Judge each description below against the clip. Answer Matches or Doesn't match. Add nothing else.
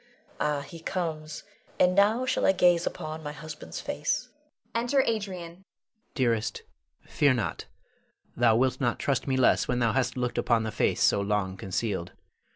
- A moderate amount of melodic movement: Doesn't match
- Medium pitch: Matches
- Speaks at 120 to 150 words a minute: Doesn't match